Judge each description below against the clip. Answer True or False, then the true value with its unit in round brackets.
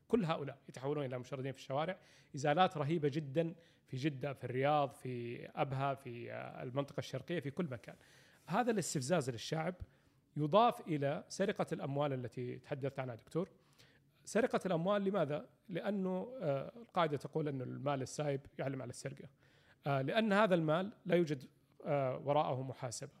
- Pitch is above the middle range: False (145 Hz)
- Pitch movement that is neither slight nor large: True (4.1 semitones)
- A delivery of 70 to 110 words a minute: False (135 wpm)